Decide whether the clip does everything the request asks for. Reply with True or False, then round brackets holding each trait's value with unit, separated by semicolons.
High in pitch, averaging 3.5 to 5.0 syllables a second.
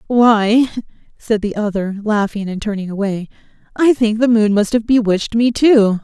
True (215 Hz; 4.8 syllables/s)